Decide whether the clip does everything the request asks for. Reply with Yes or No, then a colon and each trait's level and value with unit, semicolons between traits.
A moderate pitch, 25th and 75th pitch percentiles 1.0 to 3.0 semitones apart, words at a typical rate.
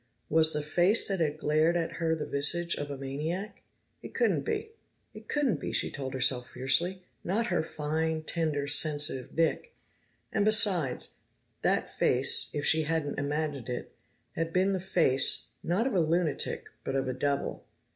No: medium, 160 Hz; average, 3.9 semitones; average, 165 wpm